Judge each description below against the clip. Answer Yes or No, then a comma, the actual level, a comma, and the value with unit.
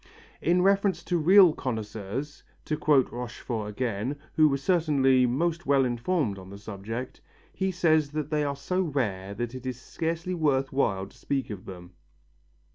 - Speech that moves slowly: No, average, 165 wpm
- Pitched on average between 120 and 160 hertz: Yes, low, 135 Hz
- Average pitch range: No, wide, 5.9 semitones